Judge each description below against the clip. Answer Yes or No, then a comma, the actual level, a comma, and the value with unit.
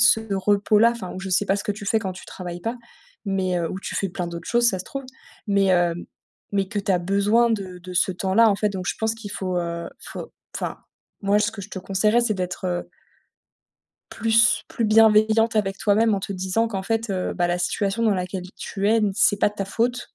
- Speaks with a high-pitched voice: Yes, high, 200 Hz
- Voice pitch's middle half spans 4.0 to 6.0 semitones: No, average, 3.0 semitones